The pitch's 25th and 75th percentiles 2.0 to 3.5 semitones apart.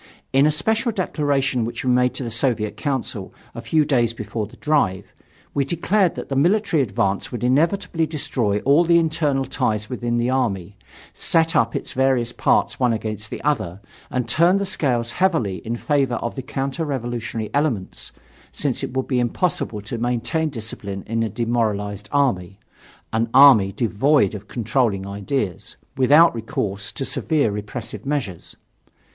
No: average, 5.0 semitones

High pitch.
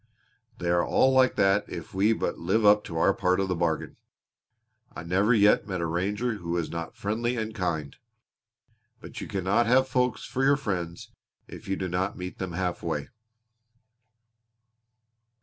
No: very low, 95 Hz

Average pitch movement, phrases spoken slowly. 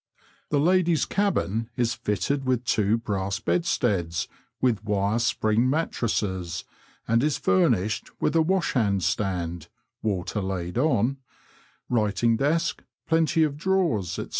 No: wide, 6.9 semitones; slow, 115 wpm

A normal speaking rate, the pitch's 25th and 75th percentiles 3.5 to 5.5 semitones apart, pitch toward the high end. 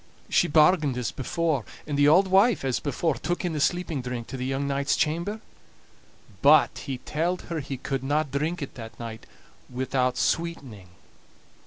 No: average, 165 wpm; average, 4.5 semitones; medium, 145 Hz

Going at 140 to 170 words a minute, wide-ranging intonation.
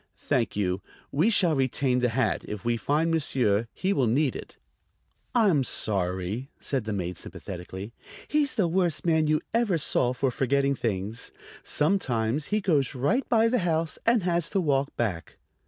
Yes: average, 165 wpm; wide, 6.9 semitones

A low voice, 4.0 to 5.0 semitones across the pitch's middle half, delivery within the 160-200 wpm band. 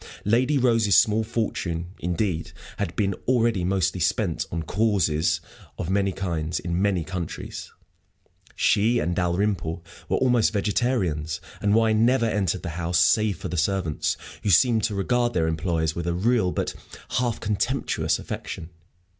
No: very low, 95 Hz; average, 4.6 semitones; average, 145 wpm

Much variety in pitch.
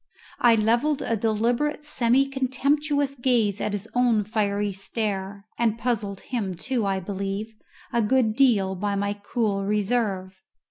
No: average, 3.6 semitones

